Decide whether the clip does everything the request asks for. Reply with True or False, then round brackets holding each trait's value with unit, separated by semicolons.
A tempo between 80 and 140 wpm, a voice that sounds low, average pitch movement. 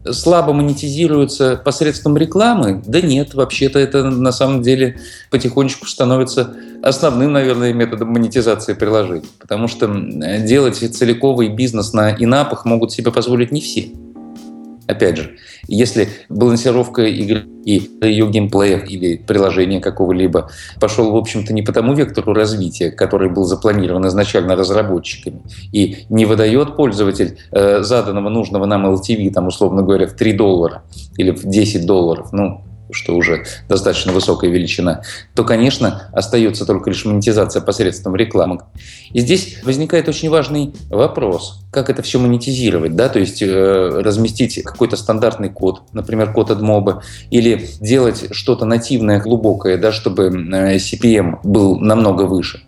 True (135 wpm; 110 Hz; 4.2 semitones)